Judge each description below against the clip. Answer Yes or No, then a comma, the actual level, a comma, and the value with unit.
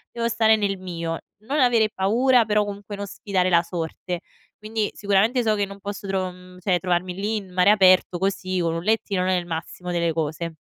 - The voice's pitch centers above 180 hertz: Yes, high, 190 Hz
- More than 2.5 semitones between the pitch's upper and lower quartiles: Yes, average, 2.9 semitones